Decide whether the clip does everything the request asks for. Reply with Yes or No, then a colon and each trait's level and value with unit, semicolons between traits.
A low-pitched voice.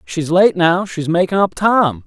No: medium, 170 Hz